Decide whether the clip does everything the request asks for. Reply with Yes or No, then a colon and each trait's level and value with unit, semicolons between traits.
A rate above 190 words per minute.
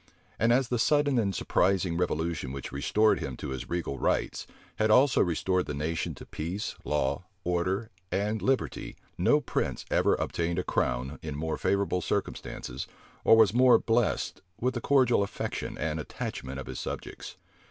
No: average, 165 wpm